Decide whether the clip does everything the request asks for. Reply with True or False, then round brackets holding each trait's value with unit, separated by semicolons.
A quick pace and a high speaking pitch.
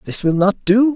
True (250 wpm; 210 Hz)